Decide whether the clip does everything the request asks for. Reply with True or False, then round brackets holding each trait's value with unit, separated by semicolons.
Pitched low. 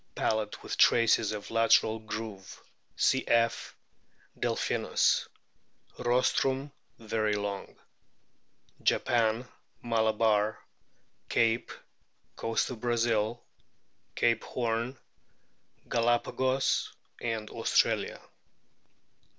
True (115 Hz)